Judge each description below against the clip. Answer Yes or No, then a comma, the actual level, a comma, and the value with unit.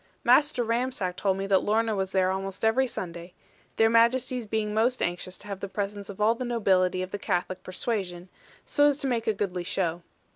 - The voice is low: No, high, 205 Hz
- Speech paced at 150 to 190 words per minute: No, fast, 205 wpm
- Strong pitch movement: No, average, 3.7 semitones